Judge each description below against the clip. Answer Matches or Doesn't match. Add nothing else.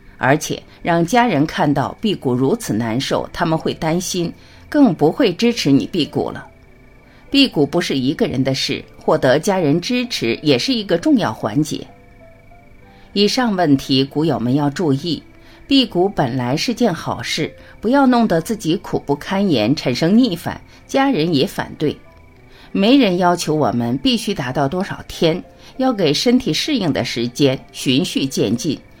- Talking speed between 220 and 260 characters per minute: Matches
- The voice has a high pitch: Doesn't match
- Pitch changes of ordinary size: Doesn't match